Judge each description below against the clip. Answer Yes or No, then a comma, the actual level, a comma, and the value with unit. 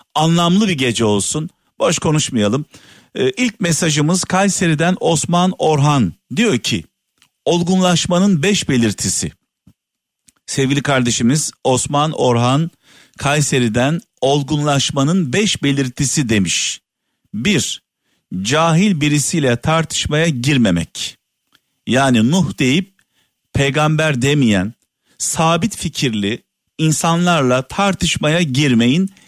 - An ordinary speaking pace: No, slow, 80 wpm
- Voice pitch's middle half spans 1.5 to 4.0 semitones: No, average, 4.7 semitones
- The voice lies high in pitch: No, medium, 150 Hz